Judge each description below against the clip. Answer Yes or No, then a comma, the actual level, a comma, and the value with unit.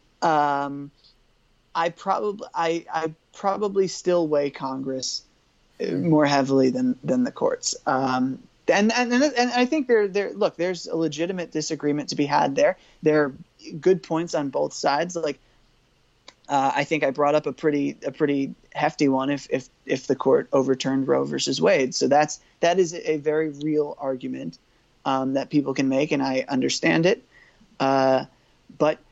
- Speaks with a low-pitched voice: No, medium, 150 Hz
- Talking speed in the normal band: Yes, average, 165 wpm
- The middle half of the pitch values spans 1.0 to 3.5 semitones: No, average, 4.2 semitones